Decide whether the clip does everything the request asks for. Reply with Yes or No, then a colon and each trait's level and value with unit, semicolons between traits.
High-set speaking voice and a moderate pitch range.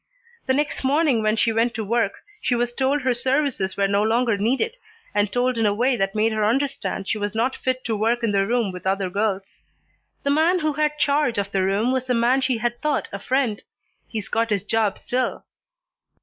Yes: high, 235 Hz; average, 4.1 semitones